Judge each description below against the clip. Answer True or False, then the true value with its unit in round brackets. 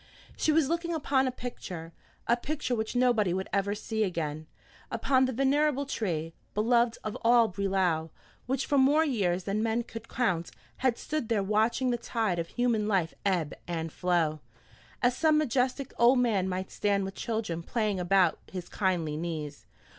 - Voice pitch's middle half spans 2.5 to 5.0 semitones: False (5.6 semitones)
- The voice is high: True (215 Hz)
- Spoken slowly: False (170 wpm)